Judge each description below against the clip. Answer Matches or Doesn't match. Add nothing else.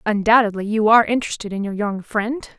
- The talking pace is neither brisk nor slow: Matches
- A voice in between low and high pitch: Doesn't match